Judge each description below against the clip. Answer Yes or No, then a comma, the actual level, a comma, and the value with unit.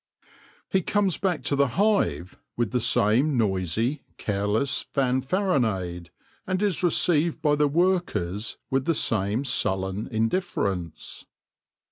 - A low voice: Yes, low, 130 Hz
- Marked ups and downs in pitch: Yes, wide, 8.7 semitones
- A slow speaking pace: Yes, slow, 115 wpm